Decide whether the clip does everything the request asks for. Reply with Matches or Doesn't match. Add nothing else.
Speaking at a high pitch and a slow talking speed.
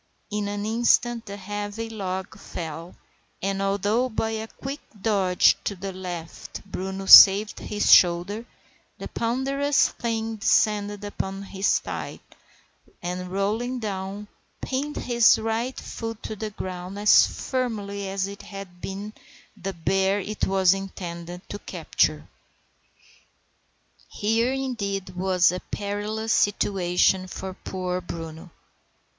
Matches